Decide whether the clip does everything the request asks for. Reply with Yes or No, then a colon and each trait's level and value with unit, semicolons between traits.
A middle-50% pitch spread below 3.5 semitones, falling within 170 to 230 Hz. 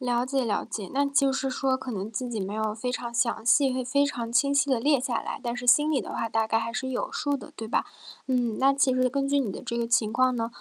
No: average, 2.8 semitones; very high, 250 Hz